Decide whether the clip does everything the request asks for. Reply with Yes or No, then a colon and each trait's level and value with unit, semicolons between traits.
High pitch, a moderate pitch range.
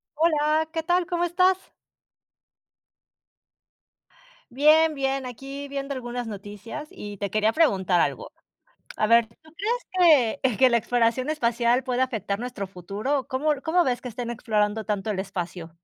No: very high, 250 Hz; wide, 5.9 semitones